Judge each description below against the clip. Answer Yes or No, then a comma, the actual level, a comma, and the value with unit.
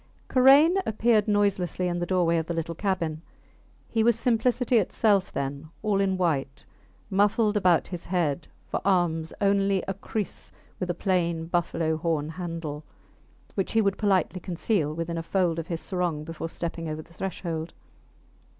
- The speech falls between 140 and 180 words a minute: Yes, average, 160 wpm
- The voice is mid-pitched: Yes, medium, 180 Hz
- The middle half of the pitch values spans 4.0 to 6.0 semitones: No, average, 3.4 semitones